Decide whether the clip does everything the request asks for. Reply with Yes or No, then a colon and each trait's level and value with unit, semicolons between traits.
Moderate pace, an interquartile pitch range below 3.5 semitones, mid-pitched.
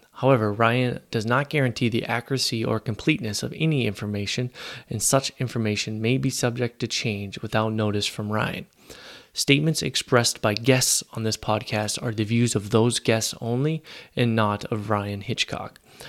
No: average, 160 wpm; average, 2.9 semitones; low, 115 Hz